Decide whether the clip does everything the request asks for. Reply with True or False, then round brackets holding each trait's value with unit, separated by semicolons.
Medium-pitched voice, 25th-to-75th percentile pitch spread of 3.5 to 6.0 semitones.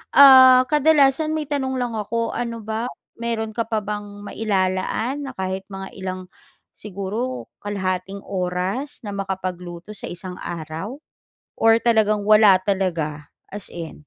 False (205 Hz; 3.9 semitones)